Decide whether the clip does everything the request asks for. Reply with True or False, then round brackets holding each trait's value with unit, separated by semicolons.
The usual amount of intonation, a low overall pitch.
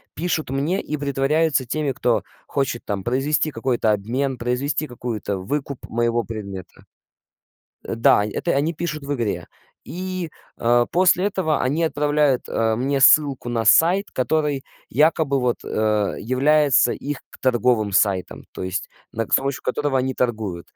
True (4.5 semitones; 130 Hz)